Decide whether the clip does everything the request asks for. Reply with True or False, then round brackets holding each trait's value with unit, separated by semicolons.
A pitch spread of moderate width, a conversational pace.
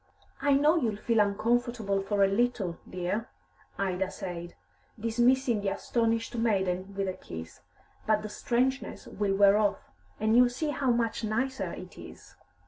True (3.6 semitones; 150 wpm)